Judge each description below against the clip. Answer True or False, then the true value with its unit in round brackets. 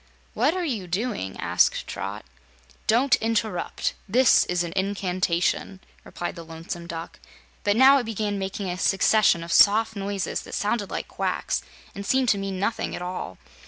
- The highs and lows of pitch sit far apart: False (4.0 semitones)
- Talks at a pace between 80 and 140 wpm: False (160 wpm)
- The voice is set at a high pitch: True (200 Hz)